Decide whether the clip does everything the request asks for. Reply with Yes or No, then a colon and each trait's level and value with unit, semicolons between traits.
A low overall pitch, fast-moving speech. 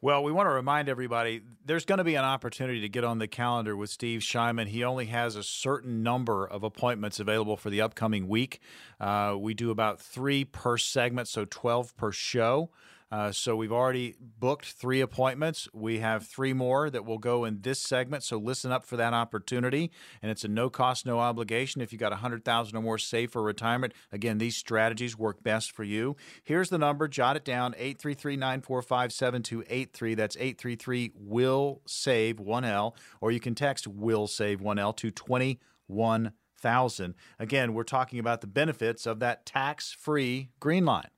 No: low, 120 Hz; average, 180 wpm